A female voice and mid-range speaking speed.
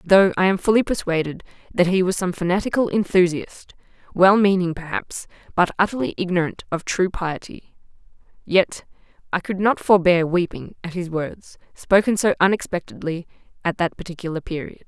Yes: female; average, 145 wpm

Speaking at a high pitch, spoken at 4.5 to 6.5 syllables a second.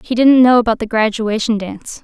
Yes: high, 225 Hz; 5.7 syllables/s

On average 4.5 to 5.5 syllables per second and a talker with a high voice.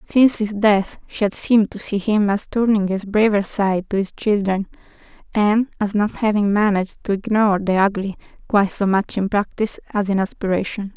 Yes: 5.4 syllables/s; high, 205 Hz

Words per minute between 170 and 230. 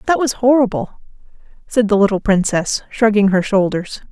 No: average, 145 wpm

